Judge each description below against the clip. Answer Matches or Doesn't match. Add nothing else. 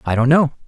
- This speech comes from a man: Matches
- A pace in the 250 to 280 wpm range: Matches